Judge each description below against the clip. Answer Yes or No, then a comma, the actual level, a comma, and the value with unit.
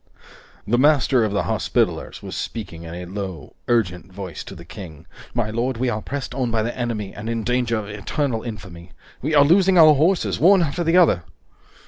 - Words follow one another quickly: No, average, 195 wpm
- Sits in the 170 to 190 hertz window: No, low, 115 Hz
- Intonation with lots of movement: Yes, wide, 6.2 semitones